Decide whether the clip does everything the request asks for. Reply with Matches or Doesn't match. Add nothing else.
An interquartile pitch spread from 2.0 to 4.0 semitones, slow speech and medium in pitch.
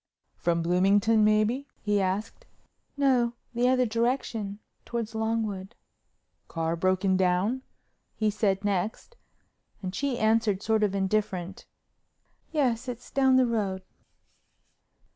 Doesn't match